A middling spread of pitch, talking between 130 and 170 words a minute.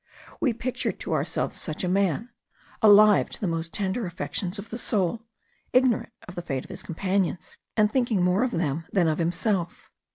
No: average, 4.3 semitones; average, 185 wpm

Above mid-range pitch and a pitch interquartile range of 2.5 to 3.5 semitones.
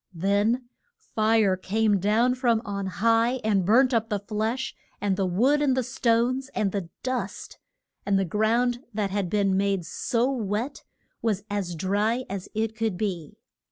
Yes: high, 215 Hz; average, 3.2 semitones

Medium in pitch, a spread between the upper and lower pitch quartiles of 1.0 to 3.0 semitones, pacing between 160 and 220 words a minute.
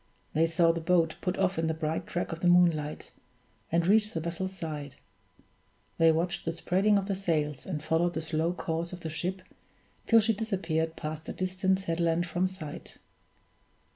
Yes: medium, 170 Hz; narrow, 2.5 semitones; average, 180 wpm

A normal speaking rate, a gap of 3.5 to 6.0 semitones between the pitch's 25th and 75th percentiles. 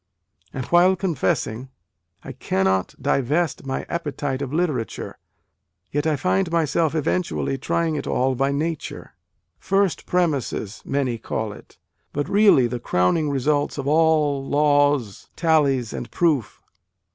No: slow, 130 wpm; average, 3.9 semitones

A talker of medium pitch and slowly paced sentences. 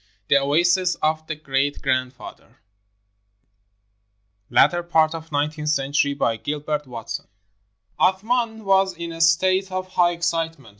Yes: medium, 160 Hz; slow, 120 wpm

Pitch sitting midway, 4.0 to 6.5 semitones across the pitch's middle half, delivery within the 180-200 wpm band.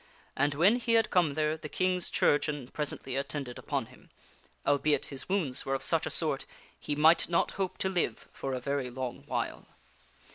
Yes: medium, 145 Hz; average, 4.4 semitones; average, 185 wpm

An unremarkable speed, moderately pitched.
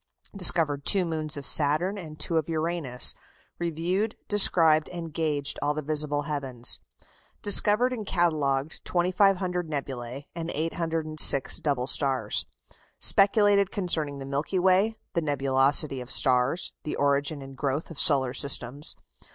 No: slow, 130 wpm; medium, 155 Hz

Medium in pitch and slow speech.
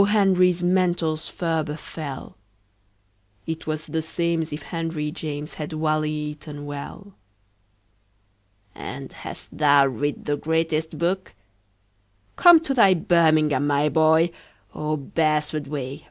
Yes: medium, 155 Hz; slow, 110 wpm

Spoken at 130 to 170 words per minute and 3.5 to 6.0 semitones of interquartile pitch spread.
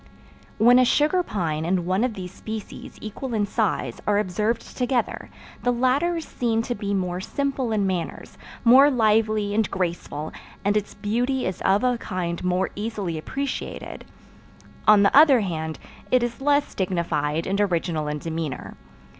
Yes: average, 160 wpm; wide, 5.4 semitones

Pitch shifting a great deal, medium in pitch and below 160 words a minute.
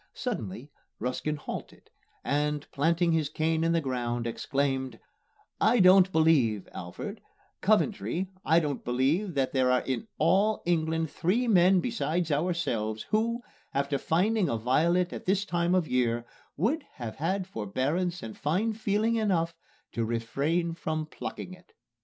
Yes: wide, 5.8 semitones; medium, 160 Hz; average, 140 wpm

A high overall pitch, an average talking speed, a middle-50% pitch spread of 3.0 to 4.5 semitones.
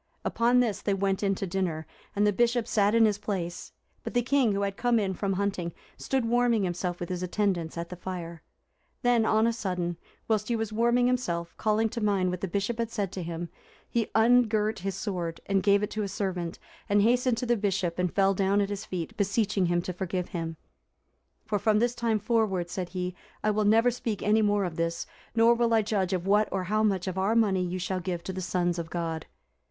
No: high, 200 Hz; fast, 225 wpm; average, 3.5 semitones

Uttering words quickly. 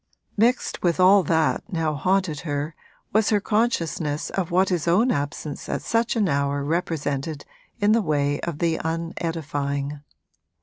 No: average, 145 wpm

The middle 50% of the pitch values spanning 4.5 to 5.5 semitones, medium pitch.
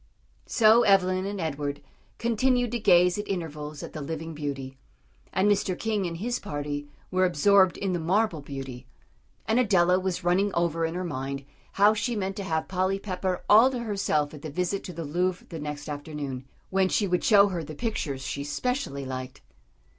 Yes: average, 5.2 semitones; medium, 180 Hz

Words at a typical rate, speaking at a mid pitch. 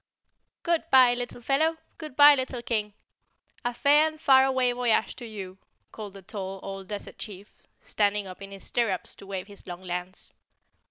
No: average, 165 wpm; high, 220 Hz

